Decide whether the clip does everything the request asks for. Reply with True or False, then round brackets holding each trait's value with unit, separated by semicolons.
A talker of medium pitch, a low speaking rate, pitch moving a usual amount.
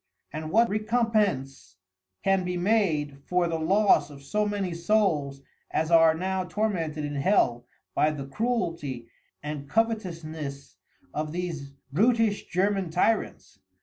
False (170 Hz; 125 wpm; 5.7 semitones)